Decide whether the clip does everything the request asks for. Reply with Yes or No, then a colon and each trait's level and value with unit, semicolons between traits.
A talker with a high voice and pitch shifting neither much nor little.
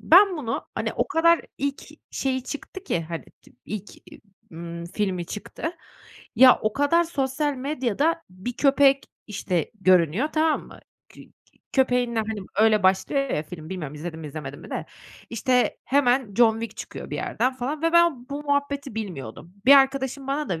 No: very high, 250 Hz; wide, 7.1 semitones